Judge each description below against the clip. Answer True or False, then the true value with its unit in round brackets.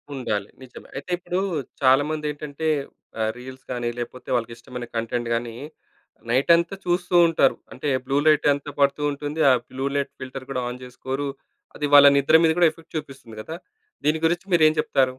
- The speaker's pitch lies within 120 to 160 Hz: True (140 Hz)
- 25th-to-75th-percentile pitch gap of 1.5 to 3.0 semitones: False (3.6 semitones)